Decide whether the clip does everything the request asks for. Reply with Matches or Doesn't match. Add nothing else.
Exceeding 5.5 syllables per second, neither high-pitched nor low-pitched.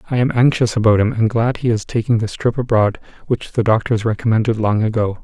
Doesn't match